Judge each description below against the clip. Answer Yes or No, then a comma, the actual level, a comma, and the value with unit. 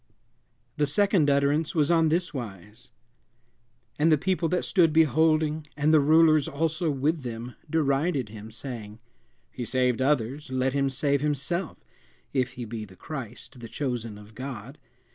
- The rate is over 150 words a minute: No, average, 145 wpm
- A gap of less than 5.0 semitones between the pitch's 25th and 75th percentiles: Yes, average, 4.2 semitones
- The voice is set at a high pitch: No, medium, 140 Hz